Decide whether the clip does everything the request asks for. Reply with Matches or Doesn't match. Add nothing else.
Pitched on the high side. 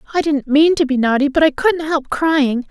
Matches